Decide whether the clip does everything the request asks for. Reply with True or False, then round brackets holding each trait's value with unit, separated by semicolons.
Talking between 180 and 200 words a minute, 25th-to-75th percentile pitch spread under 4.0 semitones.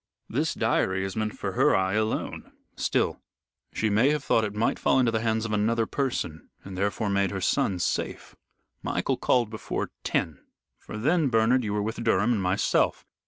True (185 wpm; 2.8 semitones)